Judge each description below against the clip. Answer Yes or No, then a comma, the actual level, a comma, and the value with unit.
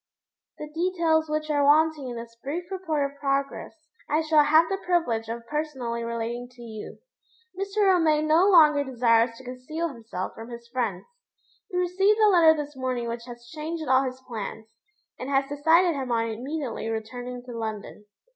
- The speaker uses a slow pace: No, average, 175 wpm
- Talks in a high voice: Yes, very high, 275 Hz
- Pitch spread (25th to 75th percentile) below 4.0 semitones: No, average, 5.2 semitones